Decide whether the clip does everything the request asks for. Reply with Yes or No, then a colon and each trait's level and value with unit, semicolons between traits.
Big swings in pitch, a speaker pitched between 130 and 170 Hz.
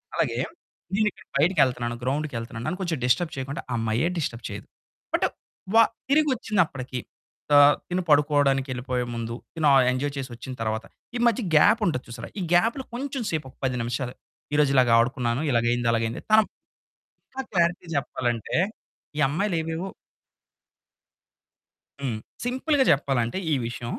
Yes: wide, 6.4 semitones; medium, 140 Hz